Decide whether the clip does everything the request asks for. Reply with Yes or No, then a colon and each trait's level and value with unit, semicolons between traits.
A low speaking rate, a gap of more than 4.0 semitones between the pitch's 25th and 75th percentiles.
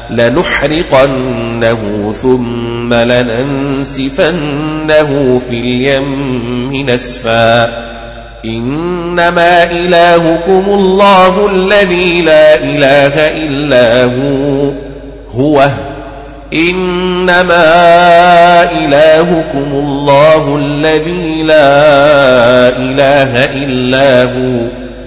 Yes: slow, 55 wpm; average, 4.9 semitones